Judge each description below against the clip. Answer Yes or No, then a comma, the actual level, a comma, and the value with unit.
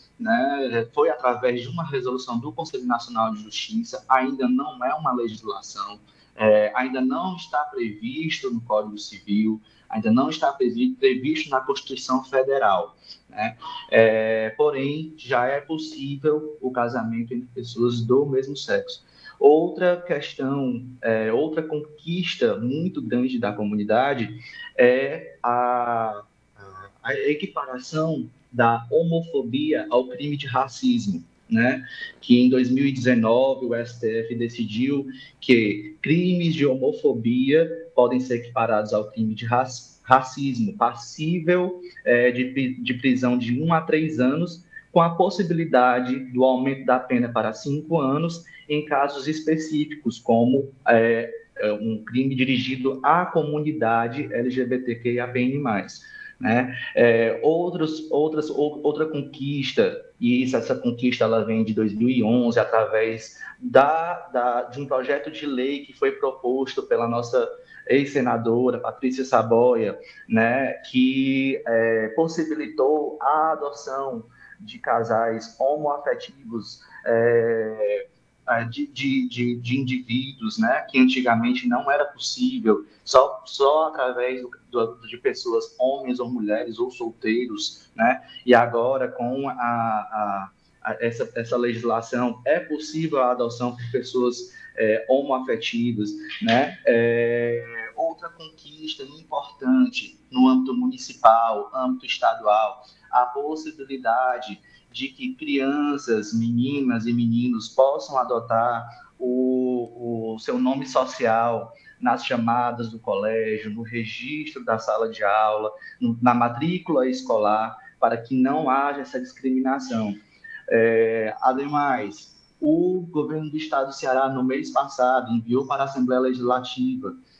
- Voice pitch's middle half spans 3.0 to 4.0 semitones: No, average, 4.9 semitones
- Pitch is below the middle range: Yes, low, 130 Hz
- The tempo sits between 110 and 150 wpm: Yes, slow, 120 wpm